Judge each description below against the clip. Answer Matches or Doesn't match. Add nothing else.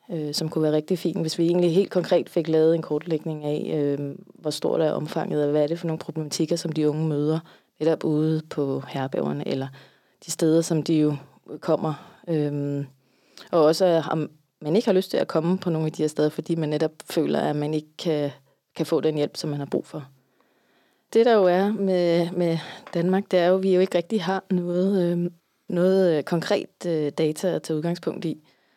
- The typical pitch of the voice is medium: Matches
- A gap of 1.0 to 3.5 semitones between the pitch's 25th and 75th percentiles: Matches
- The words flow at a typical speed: Matches